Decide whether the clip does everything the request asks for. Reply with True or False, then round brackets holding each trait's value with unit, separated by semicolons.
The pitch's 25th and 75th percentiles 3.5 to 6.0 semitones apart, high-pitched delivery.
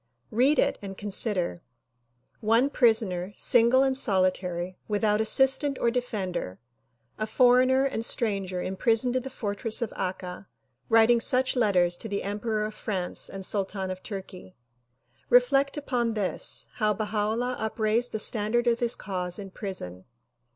True (4.0 semitones; 215 Hz)